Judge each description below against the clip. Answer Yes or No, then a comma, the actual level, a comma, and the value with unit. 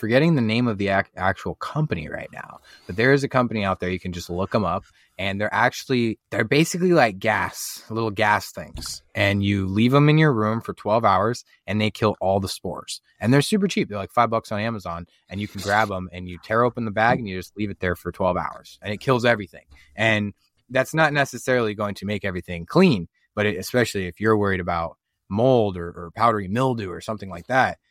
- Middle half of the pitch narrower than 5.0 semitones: Yes, average, 3.8 semitones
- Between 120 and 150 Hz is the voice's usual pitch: No, low, 105 Hz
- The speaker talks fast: Yes, fast, 230 wpm